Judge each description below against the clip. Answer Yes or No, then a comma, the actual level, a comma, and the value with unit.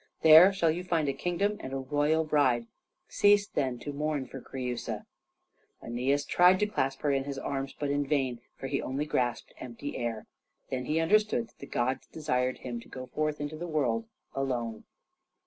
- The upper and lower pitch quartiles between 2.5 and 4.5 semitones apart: Yes, average, 3.4 semitones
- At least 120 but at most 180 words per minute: No, average, 190 wpm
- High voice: No, medium, 140 Hz